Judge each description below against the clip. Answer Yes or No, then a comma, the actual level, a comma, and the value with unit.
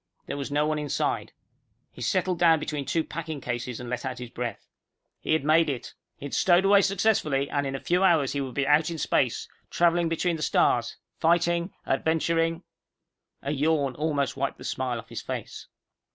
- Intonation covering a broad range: No, average, 3.6 semitones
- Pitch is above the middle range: No, medium, 150 Hz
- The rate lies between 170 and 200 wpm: Yes, average, 195 wpm